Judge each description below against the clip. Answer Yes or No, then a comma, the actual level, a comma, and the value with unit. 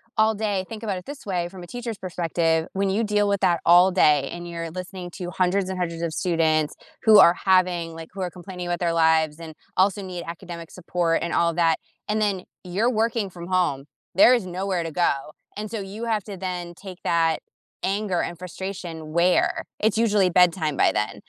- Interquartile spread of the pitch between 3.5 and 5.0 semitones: No, average, 2.8 semitones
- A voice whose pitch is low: No, medium, 180 Hz